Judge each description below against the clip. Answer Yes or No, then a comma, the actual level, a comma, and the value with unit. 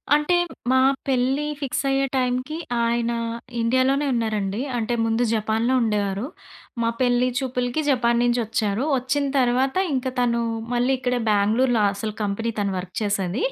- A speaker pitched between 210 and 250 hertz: Yes, high, 240 Hz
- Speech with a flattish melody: No, average, 3.0 semitones